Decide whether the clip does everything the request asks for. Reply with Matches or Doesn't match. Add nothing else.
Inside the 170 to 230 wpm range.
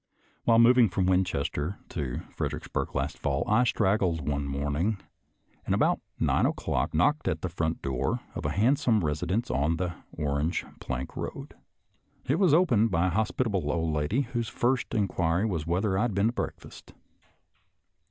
Doesn't match